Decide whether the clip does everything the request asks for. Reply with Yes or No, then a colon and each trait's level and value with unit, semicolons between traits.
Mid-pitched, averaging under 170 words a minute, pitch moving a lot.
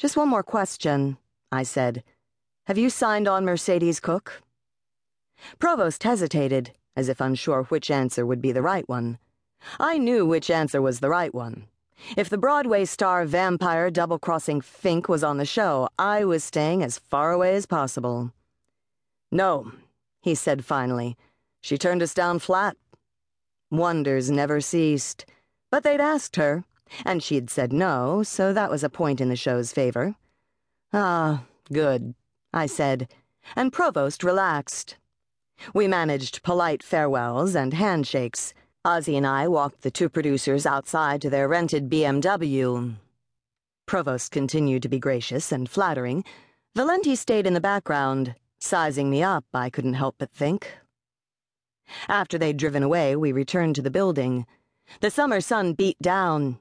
Yes: medium, 150 Hz; average, 150 wpm; wide, 5.7 semitones